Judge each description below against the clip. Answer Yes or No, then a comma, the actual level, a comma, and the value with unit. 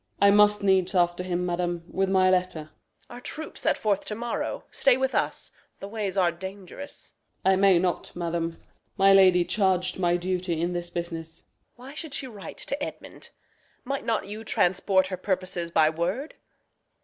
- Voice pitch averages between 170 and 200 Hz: Yes, medium, 185 Hz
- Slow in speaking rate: No, average, 185 wpm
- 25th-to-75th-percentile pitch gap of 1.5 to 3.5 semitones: Yes, average, 2.9 semitones